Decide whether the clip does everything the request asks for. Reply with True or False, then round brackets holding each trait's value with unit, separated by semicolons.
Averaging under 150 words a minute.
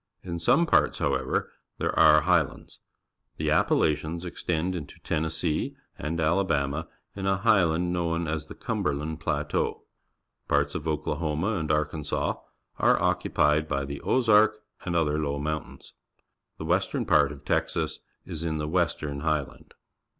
True (140 wpm)